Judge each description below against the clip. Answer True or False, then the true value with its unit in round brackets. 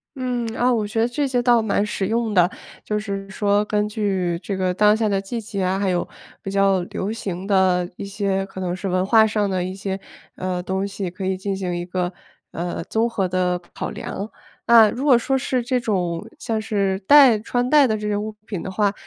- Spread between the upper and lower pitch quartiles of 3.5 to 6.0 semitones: False (2.9 semitones)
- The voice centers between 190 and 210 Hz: True (200 Hz)